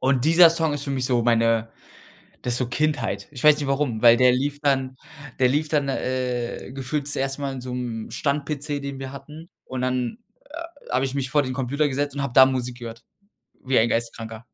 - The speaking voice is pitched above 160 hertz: No, low, 135 Hz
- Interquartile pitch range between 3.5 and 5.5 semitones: No, average, 2.7 semitones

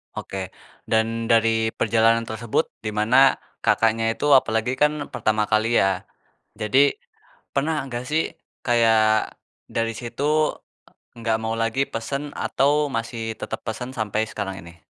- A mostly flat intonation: No, average, 3.0 semitones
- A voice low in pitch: Yes, low, 115 Hz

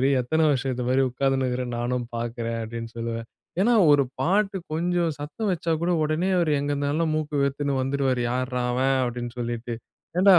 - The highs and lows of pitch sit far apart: No, average, 4.2 semitones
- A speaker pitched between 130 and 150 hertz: Yes, low, 135 Hz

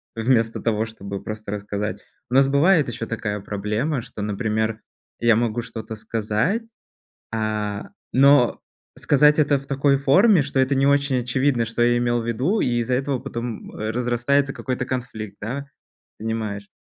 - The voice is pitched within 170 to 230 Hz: No, low, 120 Hz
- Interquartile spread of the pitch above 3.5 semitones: Yes, average, 4.0 semitones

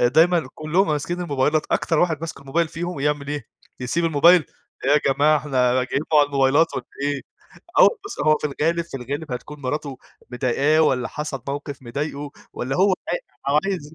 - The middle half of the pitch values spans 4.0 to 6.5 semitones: No, average, 2.8 semitones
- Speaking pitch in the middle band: Yes, medium, 145 Hz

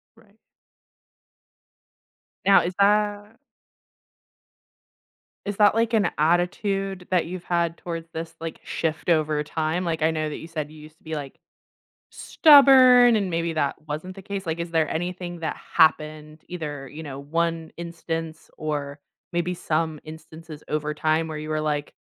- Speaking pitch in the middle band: Yes, medium, 165 Hz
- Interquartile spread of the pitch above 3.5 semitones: No, average, 2.8 semitones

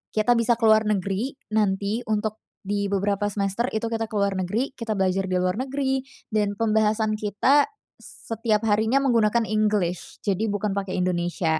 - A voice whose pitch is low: No, high, 210 Hz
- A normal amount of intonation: No, narrow, 2.2 semitones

